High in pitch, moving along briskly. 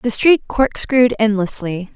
No: high, 225 Hz; slow, 125 wpm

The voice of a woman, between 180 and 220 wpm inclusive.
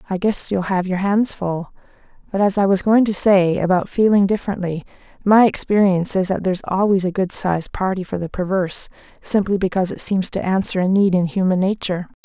Yes: female; average, 200 wpm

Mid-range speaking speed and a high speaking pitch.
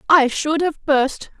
Yes: average, 170 wpm; very high, 295 Hz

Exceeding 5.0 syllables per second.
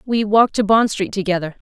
Yes: 6.0 syllables/s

